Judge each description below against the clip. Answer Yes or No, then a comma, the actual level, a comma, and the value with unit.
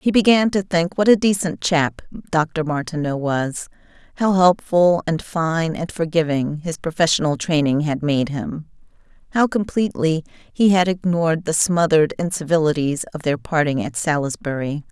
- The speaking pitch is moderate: Yes, medium, 165 Hz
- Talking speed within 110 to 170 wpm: Yes, average, 145 wpm